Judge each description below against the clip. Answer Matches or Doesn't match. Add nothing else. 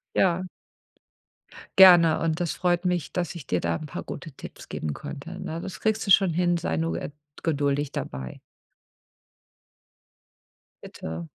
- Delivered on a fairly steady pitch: Doesn't match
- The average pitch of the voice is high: Doesn't match